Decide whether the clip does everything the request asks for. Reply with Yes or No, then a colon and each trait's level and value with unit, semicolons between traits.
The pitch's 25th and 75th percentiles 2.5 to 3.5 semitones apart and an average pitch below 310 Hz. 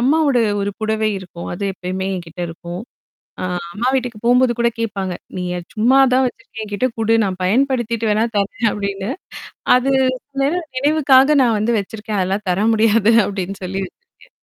No: average, 4.3 semitones; high, 220 Hz